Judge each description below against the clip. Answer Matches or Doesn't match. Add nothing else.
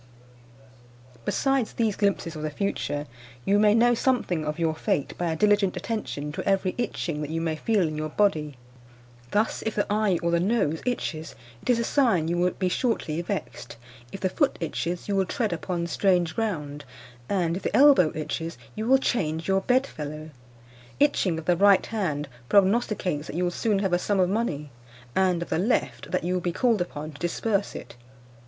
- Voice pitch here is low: Doesn't match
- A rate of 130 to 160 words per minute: Doesn't match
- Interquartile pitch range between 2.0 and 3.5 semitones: Doesn't match